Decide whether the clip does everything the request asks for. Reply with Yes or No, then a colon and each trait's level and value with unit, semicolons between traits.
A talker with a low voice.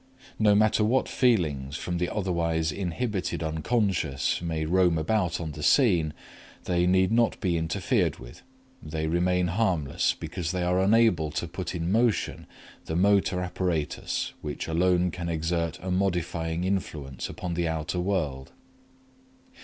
Yes: very low, 90 Hz